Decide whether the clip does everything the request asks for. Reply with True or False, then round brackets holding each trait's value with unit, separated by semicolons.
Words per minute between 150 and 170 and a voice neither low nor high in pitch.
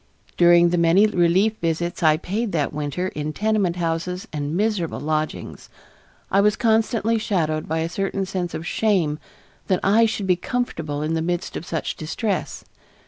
True (165 wpm; 175 Hz)